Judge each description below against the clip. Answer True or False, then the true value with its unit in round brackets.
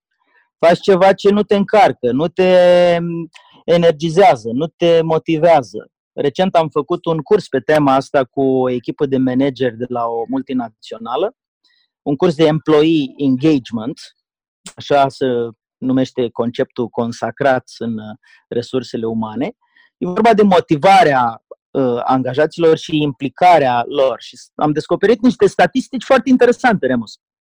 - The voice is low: False (155 Hz)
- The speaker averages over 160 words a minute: False (125 wpm)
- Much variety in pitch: True (5.9 semitones)